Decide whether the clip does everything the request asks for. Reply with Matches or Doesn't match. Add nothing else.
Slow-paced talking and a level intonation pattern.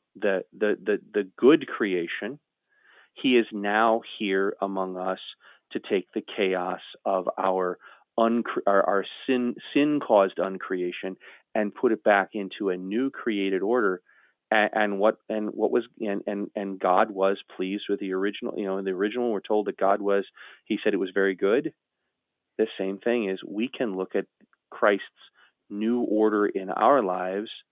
Doesn't match